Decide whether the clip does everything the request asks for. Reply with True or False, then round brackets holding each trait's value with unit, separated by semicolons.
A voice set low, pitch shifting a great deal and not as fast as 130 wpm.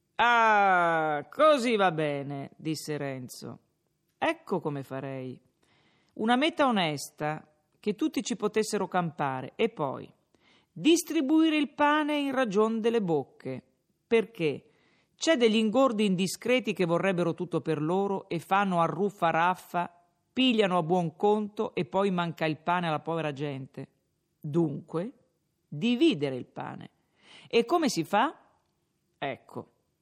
False (180 Hz; 6.5 semitones; 120 wpm)